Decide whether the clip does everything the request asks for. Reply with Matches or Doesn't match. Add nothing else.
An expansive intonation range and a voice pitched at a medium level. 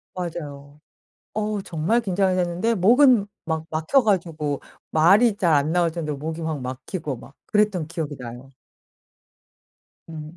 Doesn't match